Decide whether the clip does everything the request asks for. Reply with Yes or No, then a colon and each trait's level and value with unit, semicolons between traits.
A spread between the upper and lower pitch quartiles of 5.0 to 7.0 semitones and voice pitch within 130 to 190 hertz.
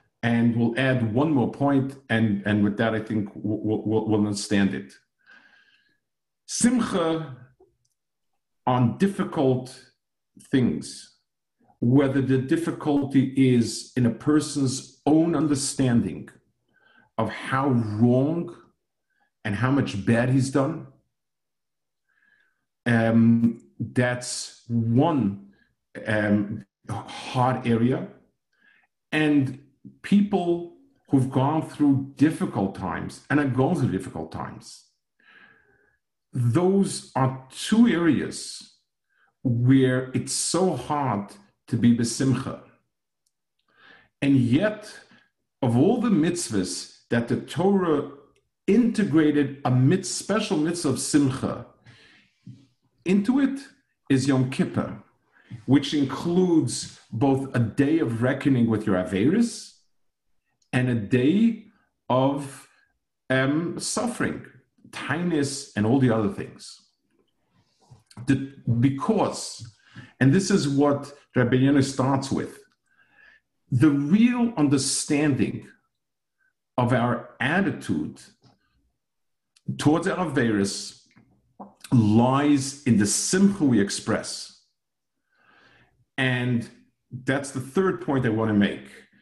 Yes: average, 5.3 semitones; low, 135 Hz